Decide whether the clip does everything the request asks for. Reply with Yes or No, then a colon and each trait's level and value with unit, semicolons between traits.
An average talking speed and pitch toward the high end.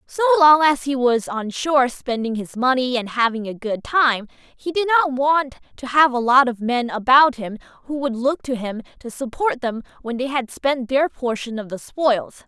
No: fast, 210 wpm; very high, 260 Hz